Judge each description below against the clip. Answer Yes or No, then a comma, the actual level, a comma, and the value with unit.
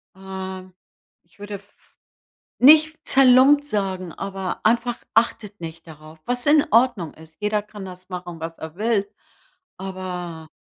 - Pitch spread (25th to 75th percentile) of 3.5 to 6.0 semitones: Yes, average, 4.6 semitones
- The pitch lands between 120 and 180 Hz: No, high, 195 Hz